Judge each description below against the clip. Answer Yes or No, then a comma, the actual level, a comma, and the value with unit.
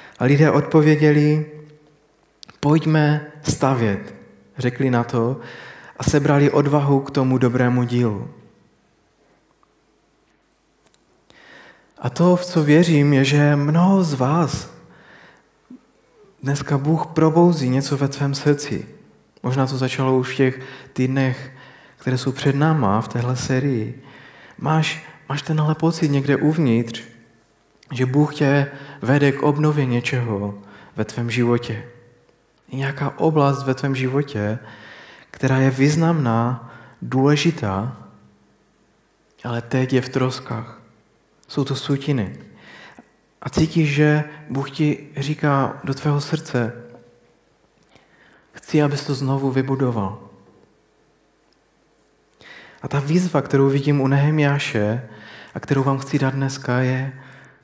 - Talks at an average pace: No, slow, 110 wpm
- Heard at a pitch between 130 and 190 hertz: Yes, low, 135 Hz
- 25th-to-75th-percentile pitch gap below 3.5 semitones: Yes, average, 3.1 semitones